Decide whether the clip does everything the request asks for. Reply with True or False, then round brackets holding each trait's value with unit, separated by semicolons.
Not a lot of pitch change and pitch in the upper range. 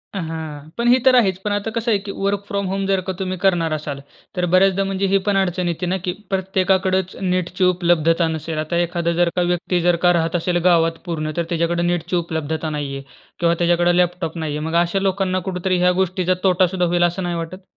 False (2.1 semitones; 180 Hz)